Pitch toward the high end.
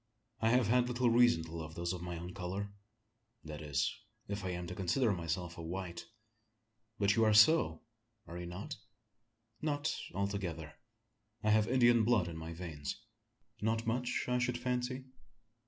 No: low, 100 Hz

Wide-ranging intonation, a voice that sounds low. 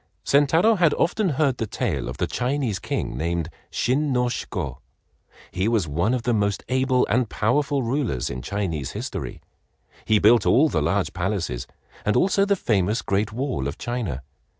Yes: wide, 6.1 semitones; low, 115 Hz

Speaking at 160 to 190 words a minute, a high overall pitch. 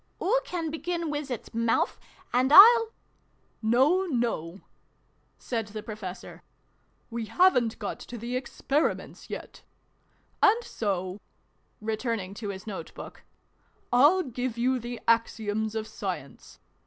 No: average, 140 wpm; high, 235 Hz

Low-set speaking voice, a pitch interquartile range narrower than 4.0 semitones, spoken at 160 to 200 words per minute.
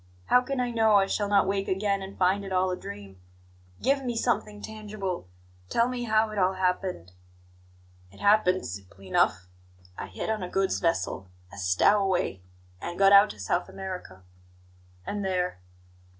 No: high, 195 Hz; average, 3.5 semitones; average, 165 wpm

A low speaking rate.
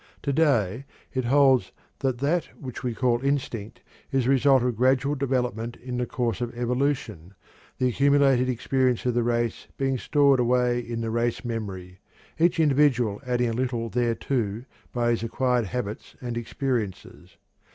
No: average, 155 wpm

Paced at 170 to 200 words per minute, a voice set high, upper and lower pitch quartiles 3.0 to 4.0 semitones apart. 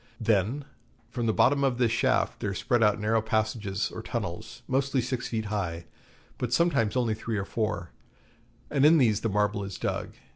No: average, 180 wpm; low, 110 Hz; average, 3.3 semitones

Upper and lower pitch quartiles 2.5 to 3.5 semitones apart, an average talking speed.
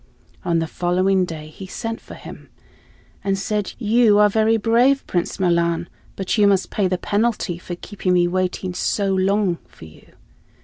Yes: average, 3.0 semitones; average, 170 wpm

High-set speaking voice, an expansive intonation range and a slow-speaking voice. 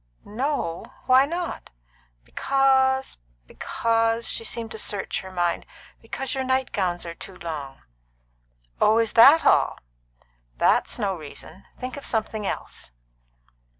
Yes: high, 225 Hz; wide, 5.9 semitones; slow, 125 wpm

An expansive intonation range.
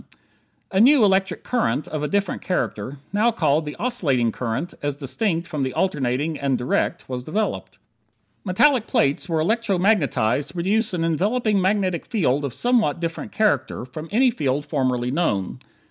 Yes: wide, 6.9 semitones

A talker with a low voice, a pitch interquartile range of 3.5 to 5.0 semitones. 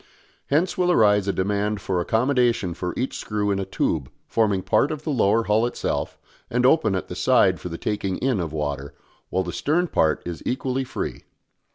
No: low, 105 Hz; wide, 5.5 semitones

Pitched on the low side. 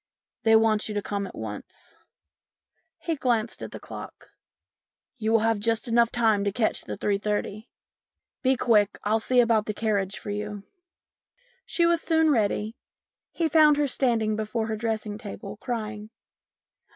No: high, 220 Hz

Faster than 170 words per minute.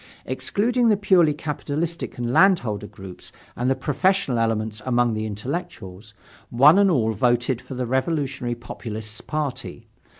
No: slow, 135 wpm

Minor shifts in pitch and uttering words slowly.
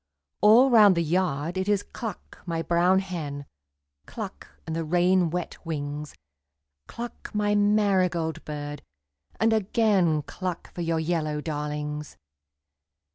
No: average, 4.4 semitones; slow, 125 wpm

